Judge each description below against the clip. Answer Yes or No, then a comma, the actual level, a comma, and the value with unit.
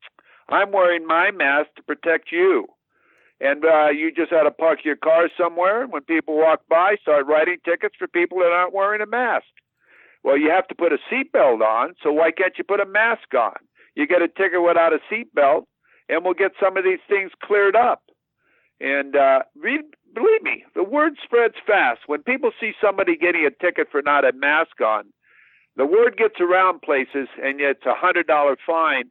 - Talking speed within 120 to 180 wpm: No, average, 200 wpm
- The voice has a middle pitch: Yes, medium, 180 Hz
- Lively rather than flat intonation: Yes, wide, 6.2 semitones